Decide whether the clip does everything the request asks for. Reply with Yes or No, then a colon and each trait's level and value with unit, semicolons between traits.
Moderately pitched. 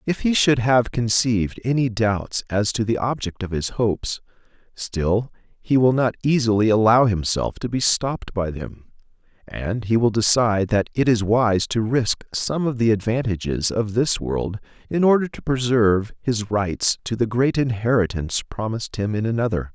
No: low, 115 Hz